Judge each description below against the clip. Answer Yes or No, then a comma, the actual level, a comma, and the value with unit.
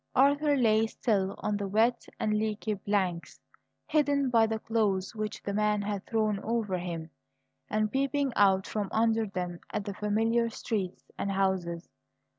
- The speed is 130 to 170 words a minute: Yes, average, 155 wpm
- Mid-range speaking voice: No, high, 210 Hz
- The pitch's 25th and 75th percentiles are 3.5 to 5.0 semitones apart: No, narrow, 2.6 semitones